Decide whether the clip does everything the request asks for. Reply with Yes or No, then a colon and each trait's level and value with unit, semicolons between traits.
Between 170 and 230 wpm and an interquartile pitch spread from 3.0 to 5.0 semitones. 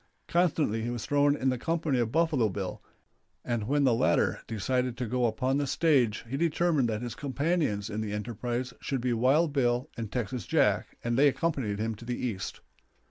Yes: average, 190 wpm; average, 4.1 semitones